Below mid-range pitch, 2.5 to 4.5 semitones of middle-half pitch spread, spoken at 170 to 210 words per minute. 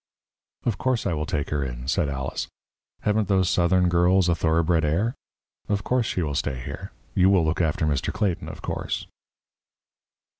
Yes: very low, 85 Hz; average, 4.2 semitones; average, 175 wpm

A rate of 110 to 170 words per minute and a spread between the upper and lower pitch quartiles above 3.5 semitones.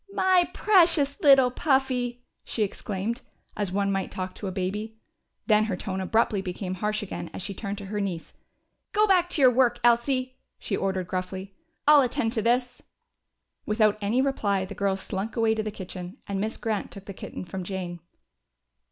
No: average, 180 wpm; average, 4.5 semitones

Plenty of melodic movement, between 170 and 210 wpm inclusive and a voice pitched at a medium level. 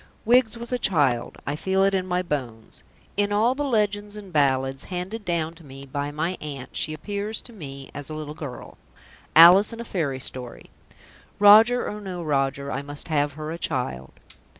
Yes: wide, 6.5 semitones; average, 190 wpm; medium, 165 Hz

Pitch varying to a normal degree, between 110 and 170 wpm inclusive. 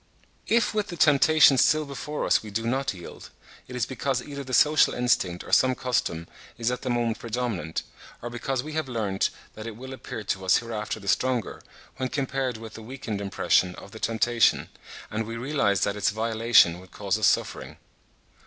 No: average, 3.7 semitones; average, 190 wpm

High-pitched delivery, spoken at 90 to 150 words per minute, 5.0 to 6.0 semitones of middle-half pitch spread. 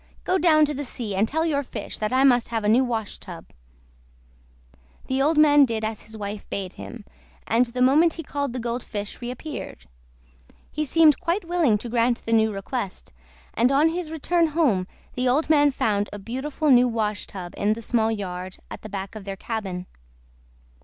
No: high, 240 Hz; average, 190 wpm; wide, 5.6 semitones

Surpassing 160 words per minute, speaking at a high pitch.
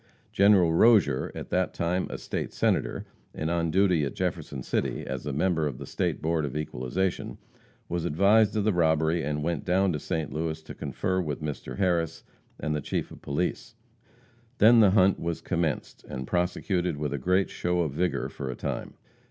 No: average, 185 wpm; very low, 85 Hz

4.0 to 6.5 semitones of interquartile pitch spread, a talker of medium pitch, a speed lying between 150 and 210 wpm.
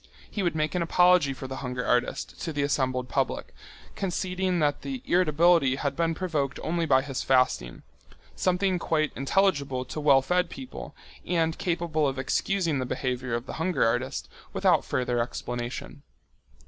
Yes: average, 5.3 semitones; medium, 150 Hz; average, 160 wpm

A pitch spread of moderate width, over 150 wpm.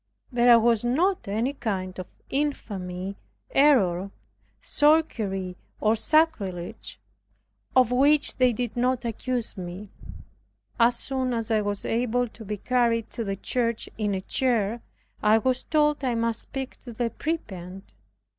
No: average, 4.0 semitones; slow, 135 wpm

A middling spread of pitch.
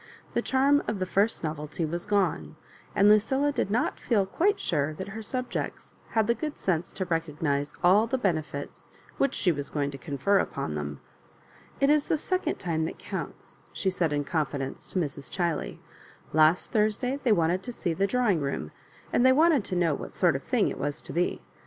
No: wide, 6.9 semitones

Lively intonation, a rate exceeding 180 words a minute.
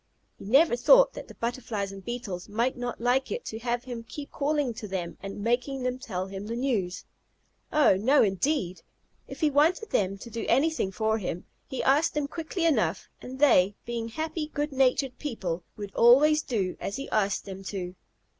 Yes: wide, 6.1 semitones; average, 190 wpm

